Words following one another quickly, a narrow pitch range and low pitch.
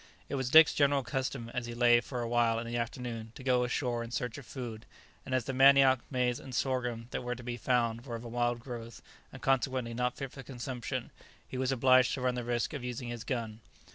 Yes: fast, 240 wpm; narrow, 1.8 semitones; low, 125 Hz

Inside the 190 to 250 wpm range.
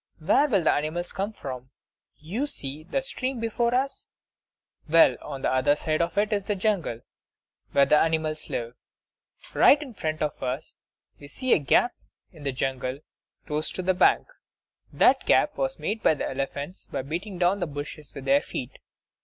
No: average, 175 wpm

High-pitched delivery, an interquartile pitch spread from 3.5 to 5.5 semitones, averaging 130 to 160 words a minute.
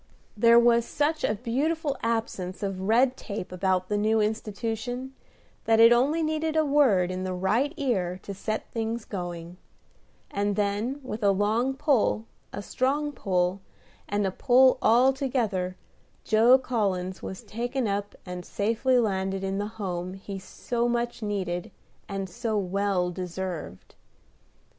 Yes: high, 215 Hz; average, 4.3 semitones; average, 145 wpm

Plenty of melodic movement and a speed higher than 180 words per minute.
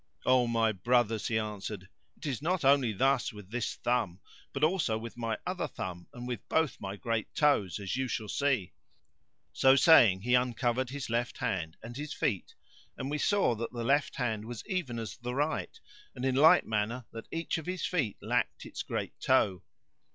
No: average, 4.2 semitones; average, 190 wpm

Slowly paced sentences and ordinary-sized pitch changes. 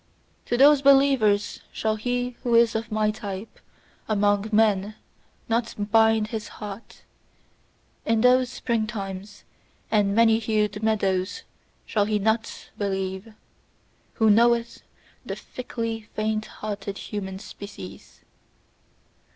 No: slow, 110 wpm; narrow, 2.1 semitones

